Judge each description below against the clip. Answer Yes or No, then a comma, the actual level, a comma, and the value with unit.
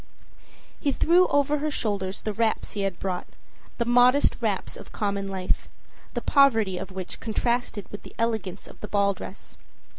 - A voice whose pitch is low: No, high, 210 Hz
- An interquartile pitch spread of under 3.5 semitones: No, average, 4.0 semitones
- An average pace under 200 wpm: Yes, average, 170 wpm